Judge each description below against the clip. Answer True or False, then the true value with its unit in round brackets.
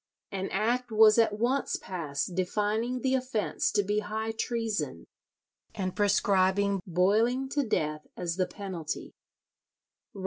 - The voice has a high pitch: True (210 Hz)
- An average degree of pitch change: True (3.4 semitones)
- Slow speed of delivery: True (125 wpm)